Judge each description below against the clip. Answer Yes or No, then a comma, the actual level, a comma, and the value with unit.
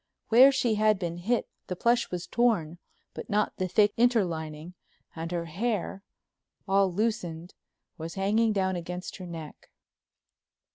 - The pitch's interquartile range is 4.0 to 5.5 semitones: Yes, average, 4.3 semitones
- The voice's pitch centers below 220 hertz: Yes, high, 190 Hz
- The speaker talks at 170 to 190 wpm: No, average, 140 wpm